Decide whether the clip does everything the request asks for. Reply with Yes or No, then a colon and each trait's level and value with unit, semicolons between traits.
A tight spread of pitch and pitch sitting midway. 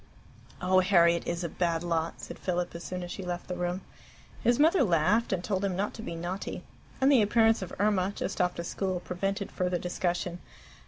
Yes: narrow, 2.3 semitones; medium, 180 Hz